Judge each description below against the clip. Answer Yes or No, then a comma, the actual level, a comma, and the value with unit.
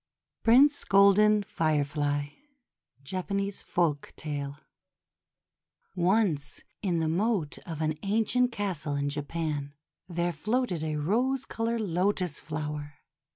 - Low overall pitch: No, medium, 170 Hz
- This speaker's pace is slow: Yes, slow, 100 wpm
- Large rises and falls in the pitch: Yes, wide, 5.8 semitones